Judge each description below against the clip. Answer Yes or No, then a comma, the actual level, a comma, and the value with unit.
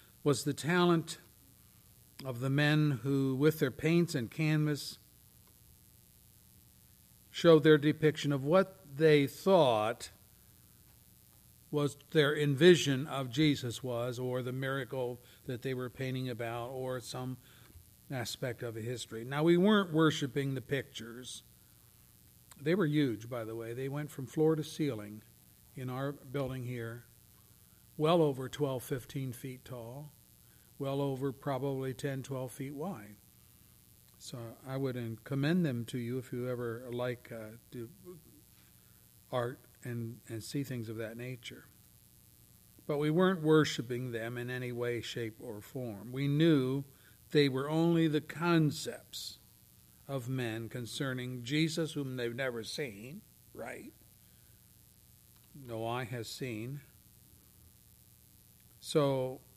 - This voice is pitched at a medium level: No, low, 130 Hz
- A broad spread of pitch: No, average, 3.7 semitones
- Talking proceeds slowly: Yes, slow, 130 wpm